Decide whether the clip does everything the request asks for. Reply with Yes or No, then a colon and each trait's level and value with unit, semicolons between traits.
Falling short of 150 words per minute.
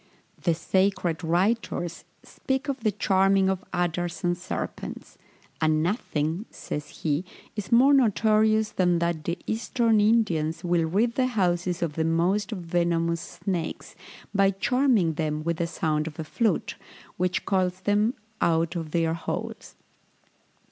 Yes: average, 140 wpm